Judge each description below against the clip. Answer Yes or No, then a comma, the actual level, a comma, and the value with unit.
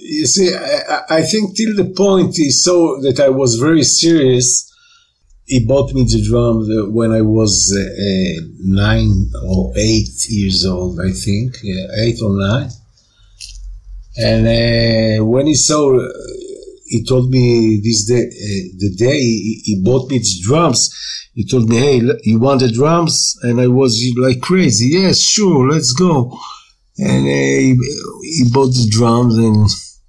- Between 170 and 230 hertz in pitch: No, low, 120 Hz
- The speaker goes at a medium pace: Yes, average, 155 wpm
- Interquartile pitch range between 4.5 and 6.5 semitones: Yes, average, 5.2 semitones